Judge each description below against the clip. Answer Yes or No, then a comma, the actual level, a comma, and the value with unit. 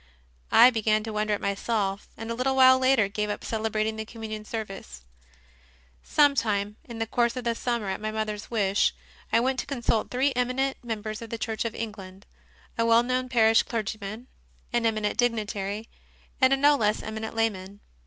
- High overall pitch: Yes, high, 220 Hz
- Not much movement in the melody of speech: Yes, narrow, 2.3 semitones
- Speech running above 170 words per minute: Yes, average, 185 wpm